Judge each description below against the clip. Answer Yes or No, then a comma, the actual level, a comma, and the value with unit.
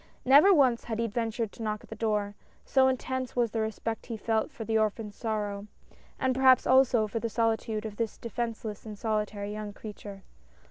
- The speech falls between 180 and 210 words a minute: Yes, average, 190 wpm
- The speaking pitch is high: Yes, high, 225 Hz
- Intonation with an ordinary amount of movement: No, narrow, 2.1 semitones